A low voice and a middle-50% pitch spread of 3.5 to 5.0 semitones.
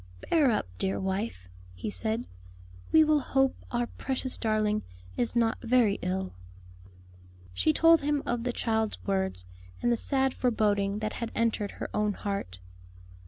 No: high, 225 Hz; average, 3.9 semitones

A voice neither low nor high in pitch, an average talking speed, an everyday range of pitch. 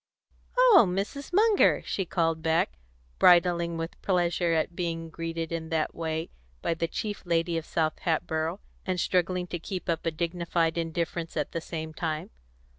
No: medium, 170 Hz; average, 160 wpm; narrow, 1.6 semitones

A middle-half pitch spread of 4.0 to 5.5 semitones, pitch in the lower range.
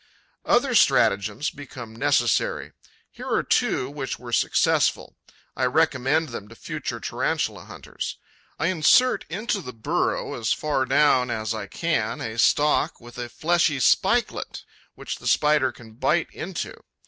Yes: average, 4.9 semitones; low, 130 Hz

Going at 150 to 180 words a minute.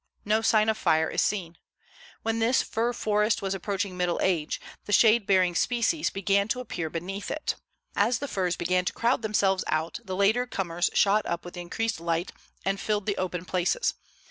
No: average, 190 wpm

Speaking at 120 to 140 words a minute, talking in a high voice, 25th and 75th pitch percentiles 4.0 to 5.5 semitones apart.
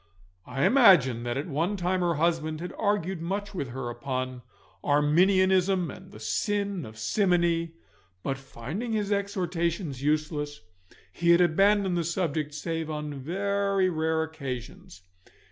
No: slow, 135 wpm; medium, 165 Hz; average, 4.7 semitones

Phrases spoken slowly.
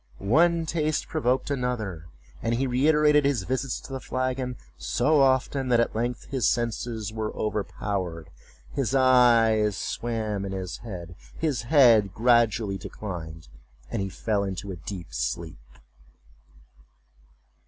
Yes: slow, 130 wpm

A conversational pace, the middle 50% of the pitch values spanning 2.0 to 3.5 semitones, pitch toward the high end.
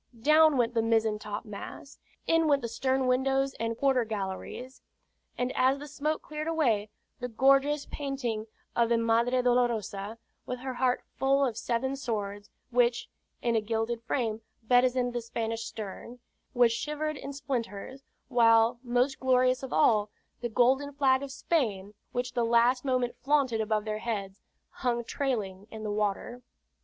Yes: average, 155 wpm; average, 3.1 semitones; high, 245 Hz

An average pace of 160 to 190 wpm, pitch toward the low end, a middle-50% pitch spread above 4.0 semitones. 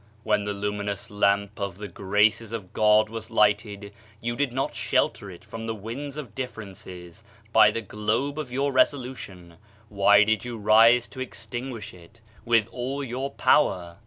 No: average, 165 wpm; low, 110 Hz; average, 3.2 semitones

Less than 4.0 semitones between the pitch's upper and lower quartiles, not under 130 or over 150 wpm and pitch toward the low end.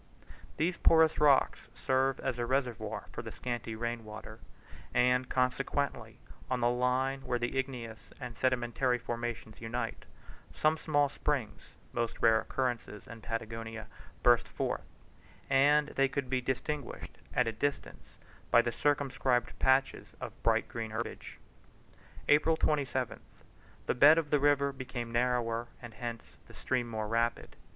Yes: narrow, 2.6 semitones; average, 145 wpm; low, 125 Hz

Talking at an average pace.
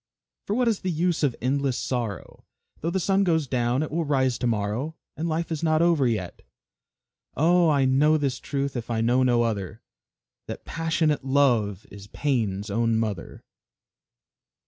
Yes: average, 170 wpm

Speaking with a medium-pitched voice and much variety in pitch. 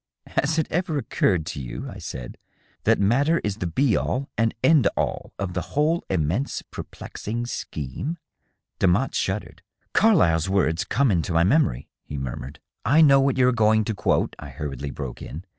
No: low, 105 Hz; wide, 9.0 semitones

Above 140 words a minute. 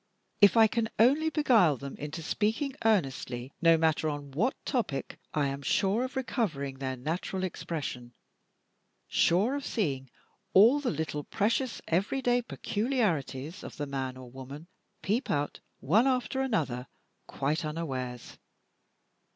No: slow, 135 wpm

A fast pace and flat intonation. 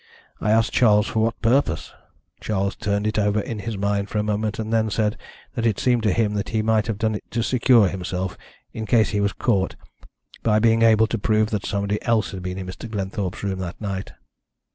Yes: fast, 220 wpm; narrow, 1.8 semitones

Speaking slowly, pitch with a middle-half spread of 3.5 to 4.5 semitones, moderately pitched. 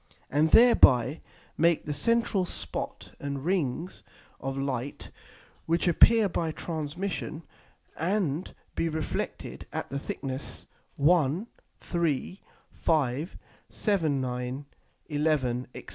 Yes: slow, 100 wpm; average, 4.2 semitones; medium, 155 Hz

